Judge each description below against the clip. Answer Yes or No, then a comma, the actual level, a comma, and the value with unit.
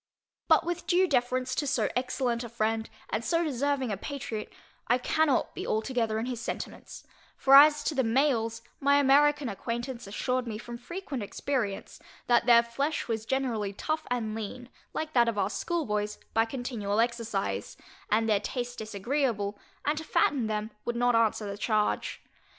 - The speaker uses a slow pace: No, average, 165 wpm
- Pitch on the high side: Yes, high, 240 Hz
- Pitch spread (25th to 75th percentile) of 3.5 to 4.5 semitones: Yes, average, 3.8 semitones